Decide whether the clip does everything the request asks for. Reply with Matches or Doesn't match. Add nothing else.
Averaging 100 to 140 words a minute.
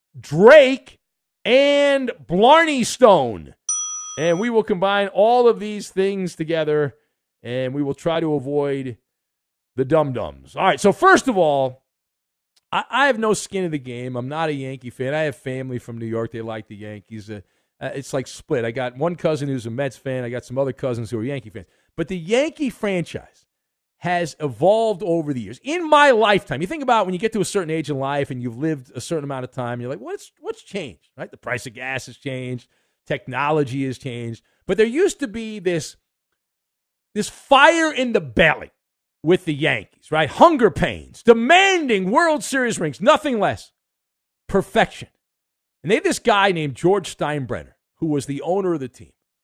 Doesn't match